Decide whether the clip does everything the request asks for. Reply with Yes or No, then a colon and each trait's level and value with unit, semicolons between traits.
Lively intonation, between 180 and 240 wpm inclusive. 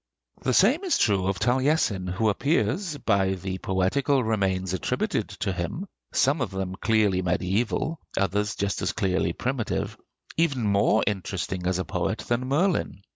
No: wide, 5.7 semitones; average, 150 wpm